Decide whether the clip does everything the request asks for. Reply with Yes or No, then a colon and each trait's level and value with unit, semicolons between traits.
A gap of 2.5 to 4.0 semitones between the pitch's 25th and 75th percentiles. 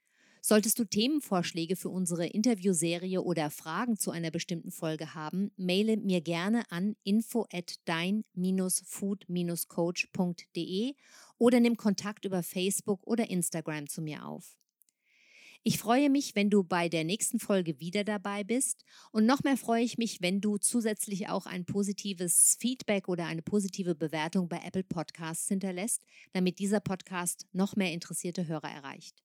Yes: average, 3.4 semitones